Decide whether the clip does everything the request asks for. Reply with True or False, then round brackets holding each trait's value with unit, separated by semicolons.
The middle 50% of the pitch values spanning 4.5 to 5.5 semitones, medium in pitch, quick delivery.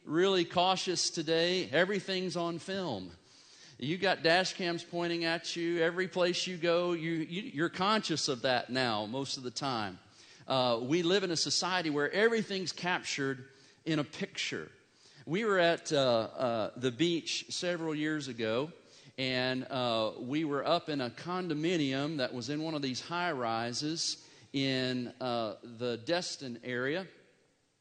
False (5.2 semitones; 155 Hz; 155 wpm)